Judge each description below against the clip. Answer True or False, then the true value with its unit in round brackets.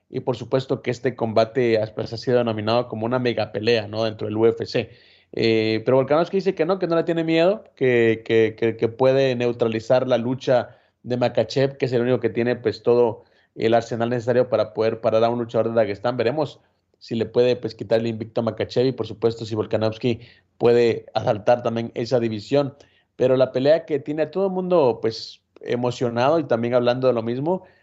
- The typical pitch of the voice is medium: False (120 Hz)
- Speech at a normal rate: False (200 wpm)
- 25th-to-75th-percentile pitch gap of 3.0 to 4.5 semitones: False (2.5 semitones)